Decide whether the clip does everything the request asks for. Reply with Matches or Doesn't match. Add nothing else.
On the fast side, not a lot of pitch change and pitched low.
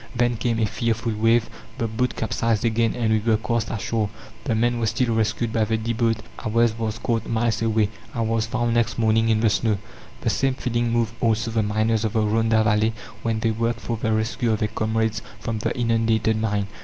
Matches